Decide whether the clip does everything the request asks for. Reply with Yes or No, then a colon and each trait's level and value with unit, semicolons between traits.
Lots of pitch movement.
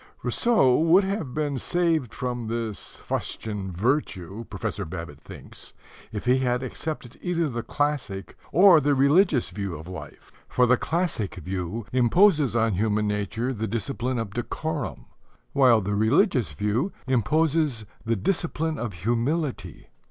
Yes: wide, 6.3 semitones